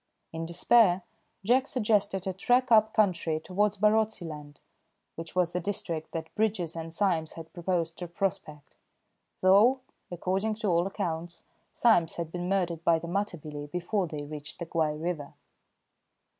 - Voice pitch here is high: No, medium, 175 Hz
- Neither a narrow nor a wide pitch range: Yes, average, 3.8 semitones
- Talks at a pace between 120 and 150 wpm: Yes, average, 145 wpm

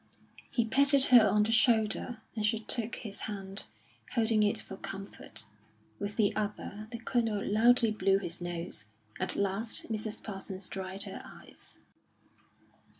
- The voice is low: No, high, 215 Hz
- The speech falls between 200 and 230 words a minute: No, average, 145 wpm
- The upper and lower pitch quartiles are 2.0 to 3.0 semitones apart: Yes, narrow, 2.5 semitones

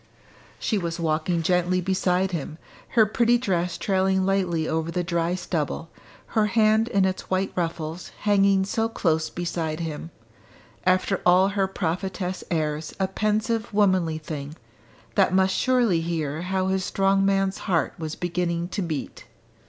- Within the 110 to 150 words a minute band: Yes, average, 145 wpm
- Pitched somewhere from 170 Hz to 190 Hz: Yes, medium, 185 Hz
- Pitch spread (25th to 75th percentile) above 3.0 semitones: No, average, 2.7 semitones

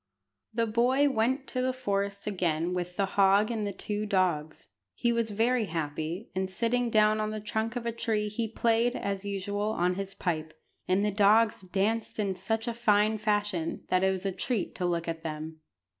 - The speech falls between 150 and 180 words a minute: No, average, 190 wpm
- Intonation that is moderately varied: Yes, average, 3.4 semitones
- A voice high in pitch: Yes, high, 205 Hz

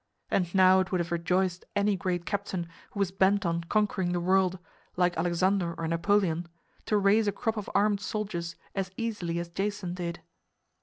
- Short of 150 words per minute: No, average, 175 wpm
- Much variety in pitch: No, average, 2.7 semitones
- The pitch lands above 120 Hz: Yes, medium, 185 Hz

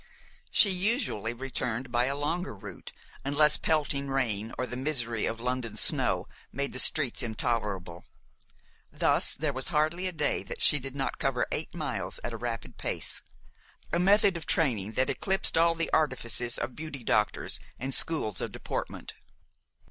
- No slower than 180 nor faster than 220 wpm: No, average, 160 wpm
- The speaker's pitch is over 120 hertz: Yes, low, 135 Hz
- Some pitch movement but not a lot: Yes, average, 4.9 semitones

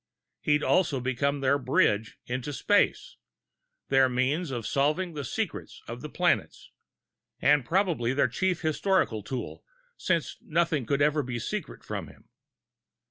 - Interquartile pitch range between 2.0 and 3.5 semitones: No, average, 4.3 semitones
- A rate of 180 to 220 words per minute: No, slow, 135 wpm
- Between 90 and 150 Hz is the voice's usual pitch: Yes, medium, 140 Hz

